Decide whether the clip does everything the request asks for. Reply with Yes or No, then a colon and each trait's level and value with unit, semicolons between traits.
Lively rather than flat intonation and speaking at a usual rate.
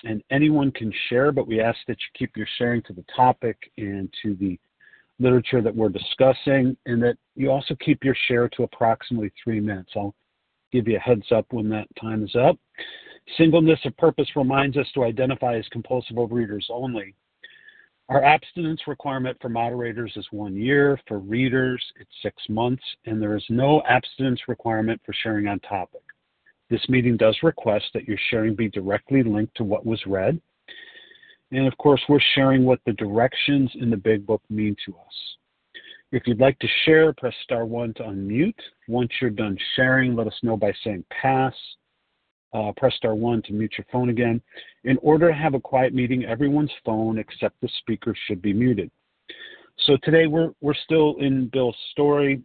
No: average, 3.7 semitones; average, 180 wpm